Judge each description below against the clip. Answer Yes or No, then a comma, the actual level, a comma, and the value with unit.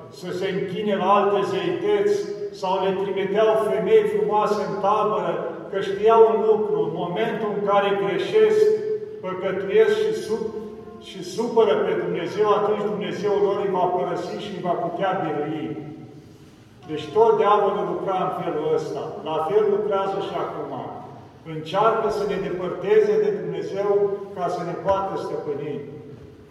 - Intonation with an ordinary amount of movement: Yes, average, 3.3 semitones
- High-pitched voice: Yes, high, 200 Hz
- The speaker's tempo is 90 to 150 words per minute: Yes, average, 145 wpm